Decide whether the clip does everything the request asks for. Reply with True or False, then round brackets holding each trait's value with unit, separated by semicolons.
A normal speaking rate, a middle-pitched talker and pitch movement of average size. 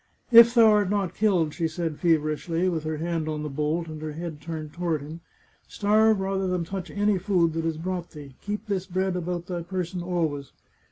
False (215 wpm; 175 Hz; 3.2 semitones)